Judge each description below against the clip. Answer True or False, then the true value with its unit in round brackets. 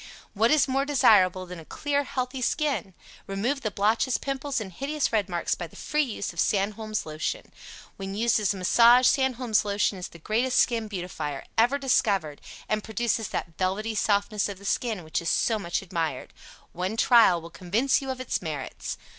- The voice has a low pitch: False (215 Hz)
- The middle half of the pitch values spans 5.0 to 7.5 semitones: True (5.3 semitones)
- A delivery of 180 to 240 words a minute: True (185 wpm)